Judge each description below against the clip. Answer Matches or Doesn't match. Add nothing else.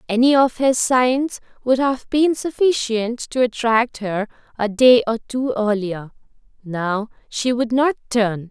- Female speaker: Matches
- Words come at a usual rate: Matches